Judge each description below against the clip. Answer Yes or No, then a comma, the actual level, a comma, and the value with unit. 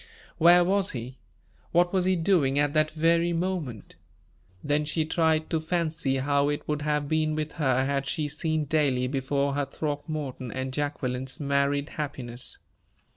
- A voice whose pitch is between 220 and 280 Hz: No, medium, 150 Hz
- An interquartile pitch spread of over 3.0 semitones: No, narrow, 2.6 semitones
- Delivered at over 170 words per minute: No, average, 155 wpm